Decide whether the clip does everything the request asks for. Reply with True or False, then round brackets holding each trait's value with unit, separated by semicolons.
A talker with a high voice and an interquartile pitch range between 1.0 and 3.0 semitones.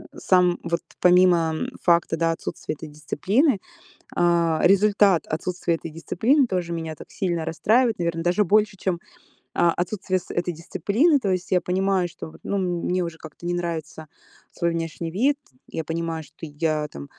False (175 Hz; 2.6 semitones)